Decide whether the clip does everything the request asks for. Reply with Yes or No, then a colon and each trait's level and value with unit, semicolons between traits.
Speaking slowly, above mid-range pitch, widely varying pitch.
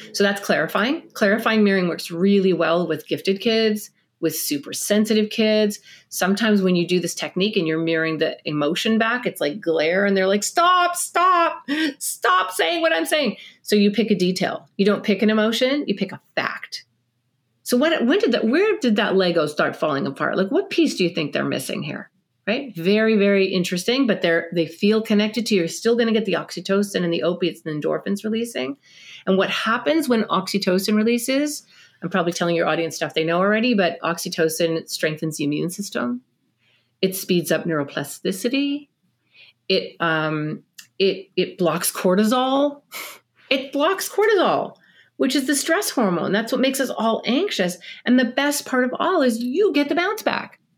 No: average, 185 wpm; high, 200 Hz; wide, 6.6 semitones